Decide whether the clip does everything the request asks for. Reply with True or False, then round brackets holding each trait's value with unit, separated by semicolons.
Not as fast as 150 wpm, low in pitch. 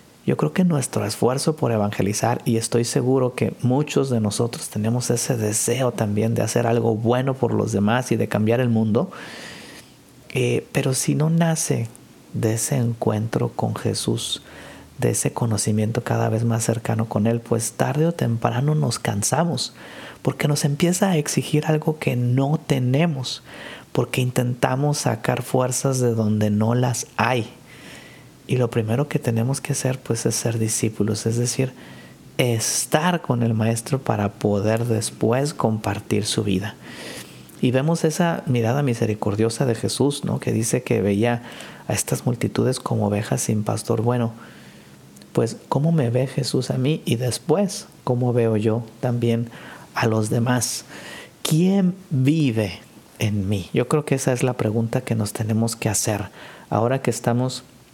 False (155 wpm; 120 Hz)